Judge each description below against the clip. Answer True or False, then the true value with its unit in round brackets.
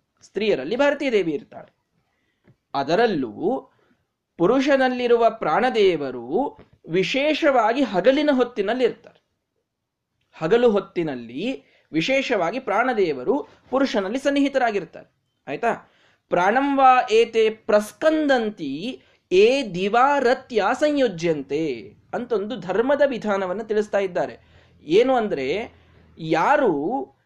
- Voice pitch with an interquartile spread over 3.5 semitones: True (5.2 semitones)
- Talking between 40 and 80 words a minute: True (70 wpm)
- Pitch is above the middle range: True (255 Hz)